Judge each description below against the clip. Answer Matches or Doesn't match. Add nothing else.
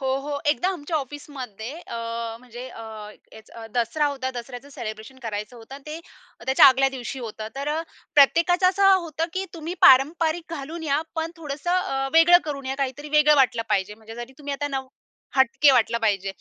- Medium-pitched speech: Doesn't match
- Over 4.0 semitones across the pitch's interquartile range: Matches